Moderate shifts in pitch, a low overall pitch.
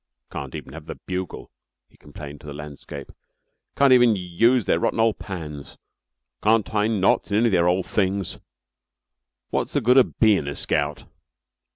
No: wide, 6.8 semitones; very low, 95 Hz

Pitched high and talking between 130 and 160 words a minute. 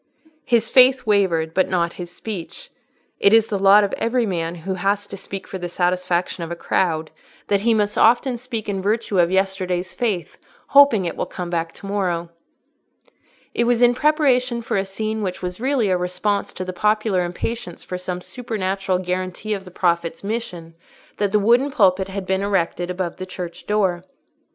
No: high, 195 Hz; average, 185 wpm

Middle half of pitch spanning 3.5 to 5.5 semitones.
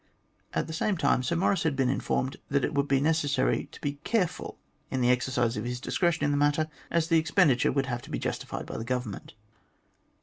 Yes: average, 4.0 semitones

